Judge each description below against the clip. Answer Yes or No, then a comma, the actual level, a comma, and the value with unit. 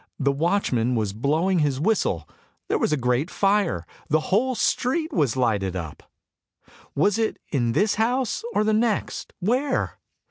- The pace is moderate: Yes, average, 150 wpm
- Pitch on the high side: No, medium, 160 Hz